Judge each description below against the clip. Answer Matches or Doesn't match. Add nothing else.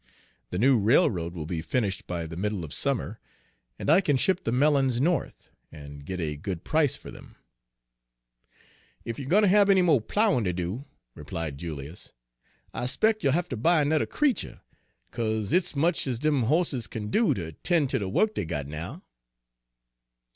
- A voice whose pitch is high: Doesn't match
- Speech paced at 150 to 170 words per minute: Doesn't match